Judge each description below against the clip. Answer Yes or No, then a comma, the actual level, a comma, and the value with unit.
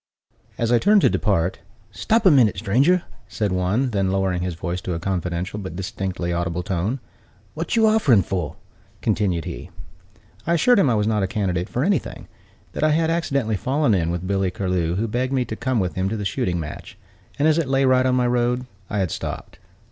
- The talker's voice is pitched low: Yes, low, 105 Hz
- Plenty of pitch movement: Yes, wide, 6.3 semitones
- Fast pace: Yes, fast, 210 wpm